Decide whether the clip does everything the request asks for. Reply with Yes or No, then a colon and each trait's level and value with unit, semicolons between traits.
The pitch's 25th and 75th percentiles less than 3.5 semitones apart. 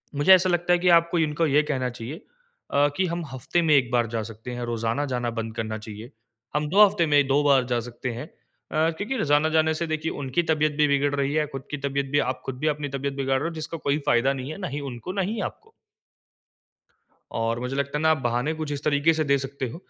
No: average, 3.8 semitones